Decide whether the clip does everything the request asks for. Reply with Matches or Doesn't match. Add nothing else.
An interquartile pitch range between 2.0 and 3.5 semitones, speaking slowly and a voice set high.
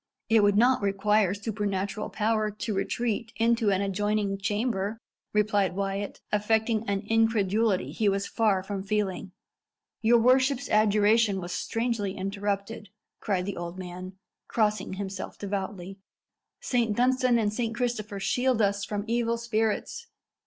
Matches